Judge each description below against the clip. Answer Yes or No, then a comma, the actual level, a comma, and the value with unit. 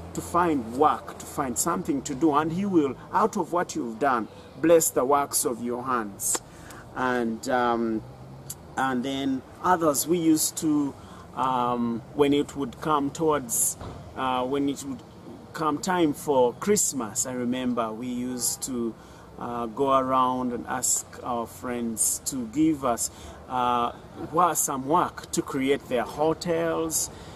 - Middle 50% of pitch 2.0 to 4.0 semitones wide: No, average, 4.6 semitones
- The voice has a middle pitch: No, low, 130 Hz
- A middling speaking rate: Yes, average, 145 wpm